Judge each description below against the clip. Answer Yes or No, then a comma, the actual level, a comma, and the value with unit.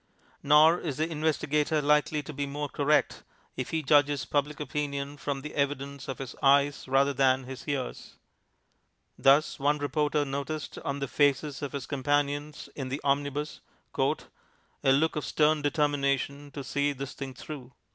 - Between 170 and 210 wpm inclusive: No, average, 155 wpm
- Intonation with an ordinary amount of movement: No, narrow, 1.3 semitones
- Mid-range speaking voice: Yes, medium, 145 Hz